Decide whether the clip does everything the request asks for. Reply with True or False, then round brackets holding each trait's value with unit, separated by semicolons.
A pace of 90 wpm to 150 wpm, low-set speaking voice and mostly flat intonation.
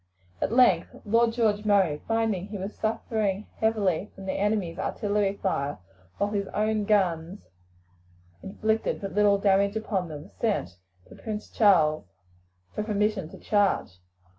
False (140 wpm; 205 Hz; 2.2 semitones)